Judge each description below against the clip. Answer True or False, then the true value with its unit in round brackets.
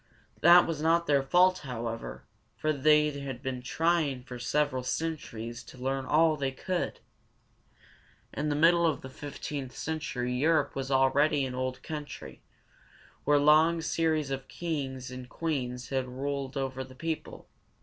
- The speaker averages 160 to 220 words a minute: False (150 wpm)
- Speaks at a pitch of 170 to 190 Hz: False (140 Hz)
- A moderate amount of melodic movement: True (3.4 semitones)